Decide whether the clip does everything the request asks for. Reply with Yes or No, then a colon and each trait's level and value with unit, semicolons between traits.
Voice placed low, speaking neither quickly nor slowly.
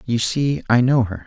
No: low, 115 Hz; fast, 235 wpm